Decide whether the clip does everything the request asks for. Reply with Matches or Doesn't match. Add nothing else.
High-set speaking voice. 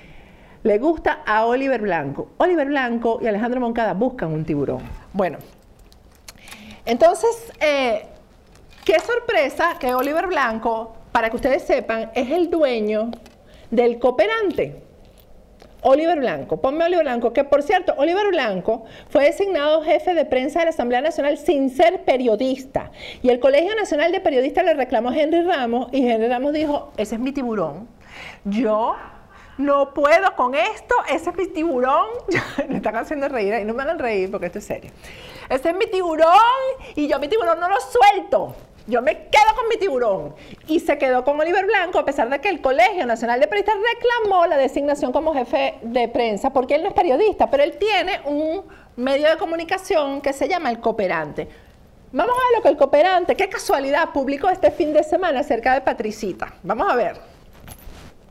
Matches